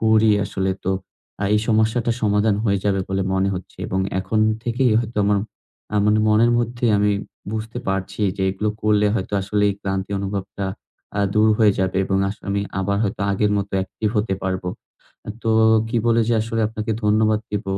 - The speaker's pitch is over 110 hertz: No, low, 105 Hz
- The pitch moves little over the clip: Yes, narrow, 2.3 semitones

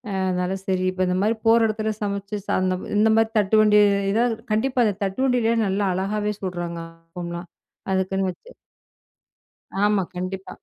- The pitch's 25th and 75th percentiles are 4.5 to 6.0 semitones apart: No, narrow, 2.5 semitones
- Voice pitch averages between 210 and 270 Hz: No, high, 200 Hz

